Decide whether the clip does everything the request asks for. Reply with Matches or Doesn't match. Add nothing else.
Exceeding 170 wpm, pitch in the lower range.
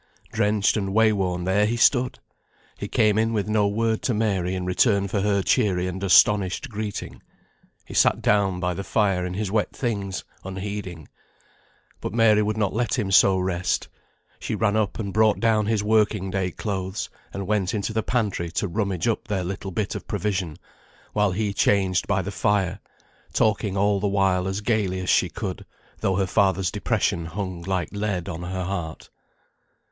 Matches